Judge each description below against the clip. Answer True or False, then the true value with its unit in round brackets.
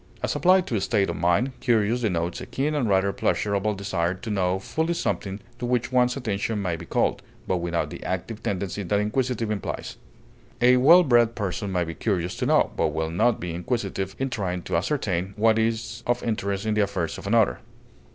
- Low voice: True (105 Hz)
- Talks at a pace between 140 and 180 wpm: False (200 wpm)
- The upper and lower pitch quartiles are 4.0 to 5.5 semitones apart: True (4.4 semitones)